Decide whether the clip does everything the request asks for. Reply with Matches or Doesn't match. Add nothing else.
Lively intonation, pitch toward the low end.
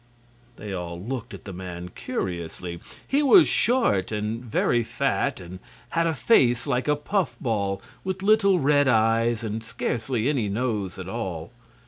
Matches